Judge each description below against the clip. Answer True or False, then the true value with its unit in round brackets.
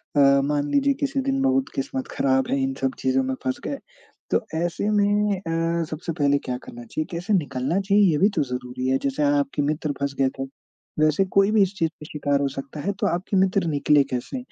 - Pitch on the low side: False (155 Hz)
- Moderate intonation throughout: False (6.5 semitones)